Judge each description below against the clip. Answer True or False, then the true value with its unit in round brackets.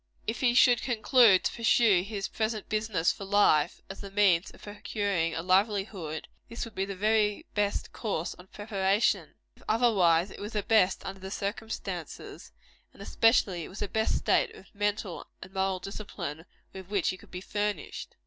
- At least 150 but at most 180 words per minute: True (175 wpm)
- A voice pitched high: True (200 Hz)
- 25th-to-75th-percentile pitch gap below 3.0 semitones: True (2.6 semitones)